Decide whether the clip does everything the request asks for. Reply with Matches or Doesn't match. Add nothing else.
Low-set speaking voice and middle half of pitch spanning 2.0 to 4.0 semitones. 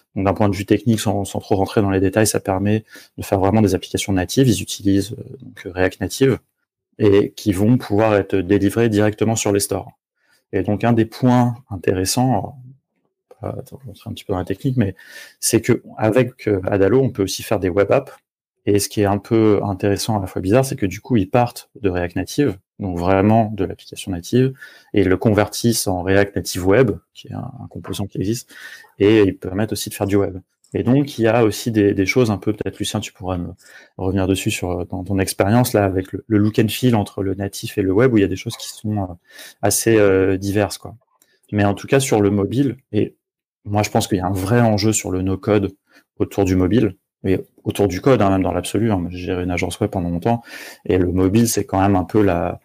Matches